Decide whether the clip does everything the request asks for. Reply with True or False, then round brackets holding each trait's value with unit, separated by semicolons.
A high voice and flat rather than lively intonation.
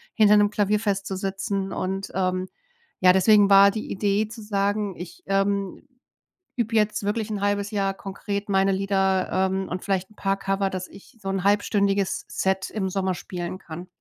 True (195 Hz; 1.2 semitones)